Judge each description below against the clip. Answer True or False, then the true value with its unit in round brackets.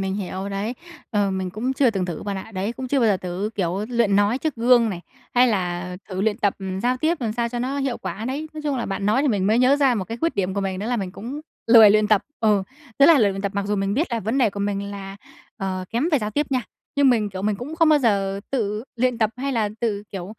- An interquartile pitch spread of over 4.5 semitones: False (4.2 semitones)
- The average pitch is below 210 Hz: False (215 Hz)